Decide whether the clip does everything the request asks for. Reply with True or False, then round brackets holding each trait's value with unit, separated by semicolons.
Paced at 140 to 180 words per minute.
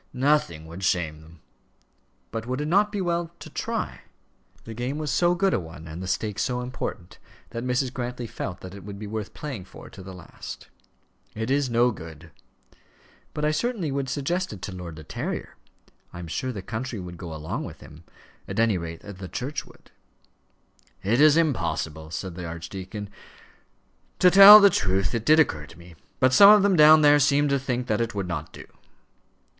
False (195 wpm)